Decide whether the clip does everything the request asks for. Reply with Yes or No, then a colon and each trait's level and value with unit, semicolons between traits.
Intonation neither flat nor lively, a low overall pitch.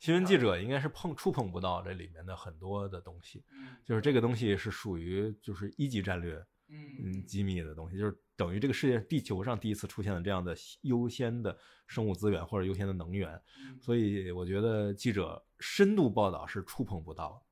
Yes: average, 4.7 semitones; low, 105 Hz